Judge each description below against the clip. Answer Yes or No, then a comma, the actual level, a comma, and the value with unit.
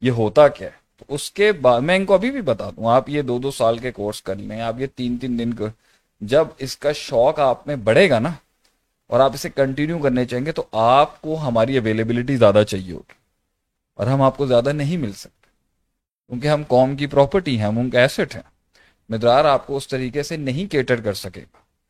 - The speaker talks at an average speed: No, fast, 225 wpm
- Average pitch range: Yes, average, 4.2 semitones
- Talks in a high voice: No, low, 130 Hz